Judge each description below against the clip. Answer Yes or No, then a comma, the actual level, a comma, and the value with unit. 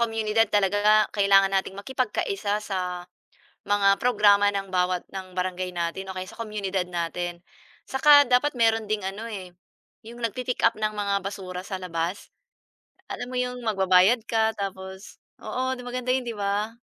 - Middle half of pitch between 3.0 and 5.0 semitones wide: Yes, average, 3.3 semitones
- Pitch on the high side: Yes, high, 205 Hz